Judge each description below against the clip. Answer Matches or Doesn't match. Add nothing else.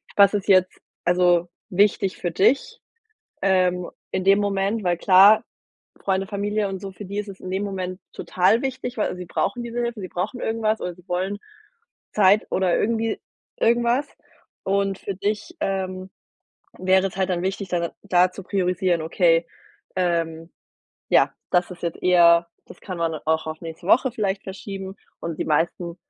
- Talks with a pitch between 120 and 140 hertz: Doesn't match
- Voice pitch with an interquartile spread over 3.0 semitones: Doesn't match